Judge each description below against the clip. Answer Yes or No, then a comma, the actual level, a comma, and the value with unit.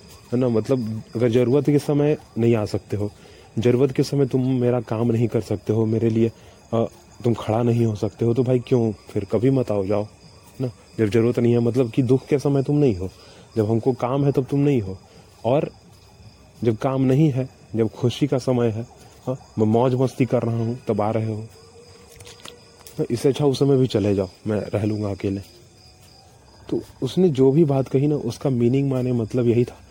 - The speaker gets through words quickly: Yes, fast, 210 wpm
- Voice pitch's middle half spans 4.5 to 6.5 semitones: No, average, 3.7 semitones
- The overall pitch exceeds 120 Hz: No, low, 115 Hz